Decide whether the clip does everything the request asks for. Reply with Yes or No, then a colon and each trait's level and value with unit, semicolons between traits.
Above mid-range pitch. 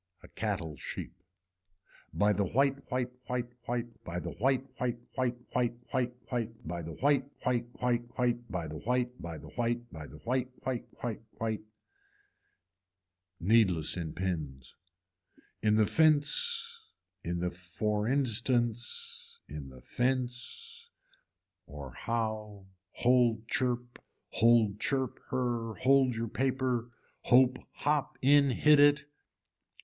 No: low, 120 Hz